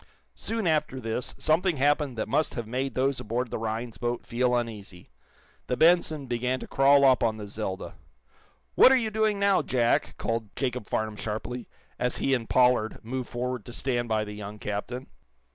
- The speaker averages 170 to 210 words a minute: Yes, average, 180 wpm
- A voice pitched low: Yes, low, 125 Hz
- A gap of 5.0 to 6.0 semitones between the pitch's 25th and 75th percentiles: No, average, 3.6 semitones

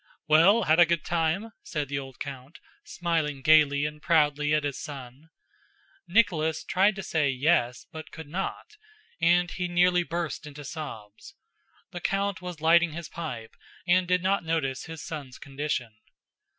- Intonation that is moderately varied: Yes, average, 3.4 semitones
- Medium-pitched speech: Yes, medium, 160 Hz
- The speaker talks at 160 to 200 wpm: No, average, 150 wpm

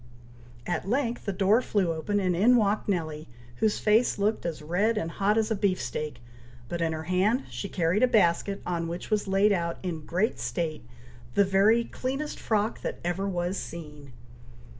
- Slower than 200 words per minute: Yes, average, 180 wpm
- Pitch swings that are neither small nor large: Yes, average, 4.1 semitones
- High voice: Yes, high, 195 Hz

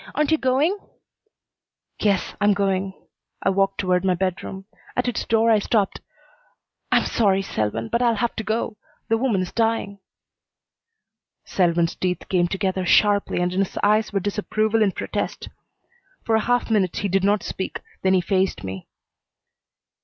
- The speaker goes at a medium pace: Yes, average, 160 wpm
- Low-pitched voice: No, high, 200 Hz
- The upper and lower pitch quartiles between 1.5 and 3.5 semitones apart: Yes, average, 2.9 semitones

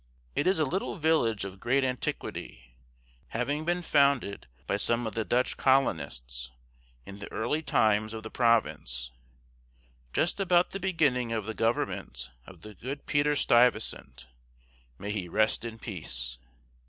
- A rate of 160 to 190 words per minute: No, average, 145 wpm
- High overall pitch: No, low, 115 Hz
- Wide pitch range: Yes, wide, 6.1 semitones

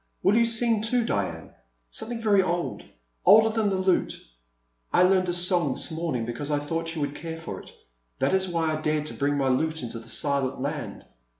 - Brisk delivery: Yes, fast, 210 wpm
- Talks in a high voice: No, medium, 165 Hz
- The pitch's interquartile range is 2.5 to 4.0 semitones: No, average, 5.2 semitones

